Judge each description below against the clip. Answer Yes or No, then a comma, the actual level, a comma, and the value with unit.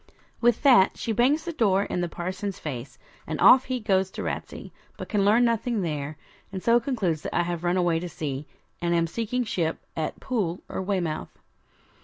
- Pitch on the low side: No, high, 190 Hz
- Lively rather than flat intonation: Yes, wide, 5.7 semitones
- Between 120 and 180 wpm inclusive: No, average, 195 wpm